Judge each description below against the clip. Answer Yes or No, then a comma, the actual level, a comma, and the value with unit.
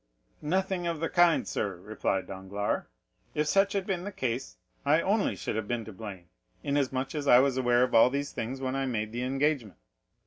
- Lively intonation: Yes, wide, 5.7 semitones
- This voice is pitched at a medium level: No, low, 130 Hz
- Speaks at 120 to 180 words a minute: No, average, 200 wpm